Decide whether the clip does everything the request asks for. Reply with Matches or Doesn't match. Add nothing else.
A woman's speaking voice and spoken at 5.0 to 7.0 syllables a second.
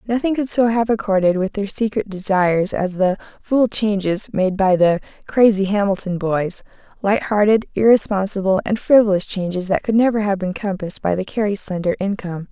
Matches